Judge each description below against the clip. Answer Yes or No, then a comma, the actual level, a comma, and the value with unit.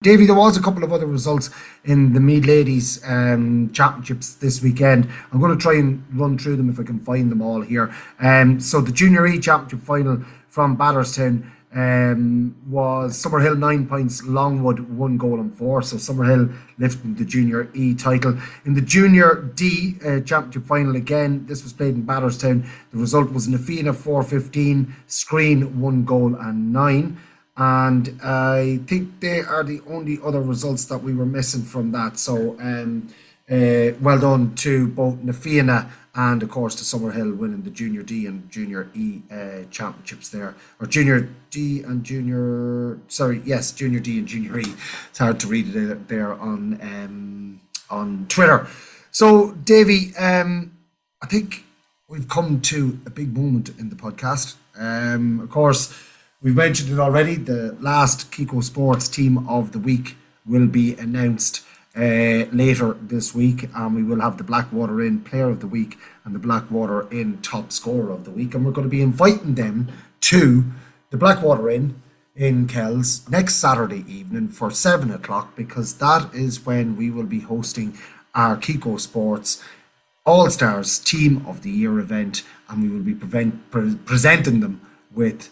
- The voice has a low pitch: Yes, low, 130 Hz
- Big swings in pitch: No, average, 3.7 semitones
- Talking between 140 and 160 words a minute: No, average, 170 wpm